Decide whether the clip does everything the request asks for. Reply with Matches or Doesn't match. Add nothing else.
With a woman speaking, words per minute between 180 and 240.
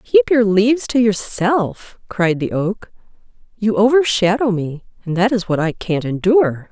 Doesn't match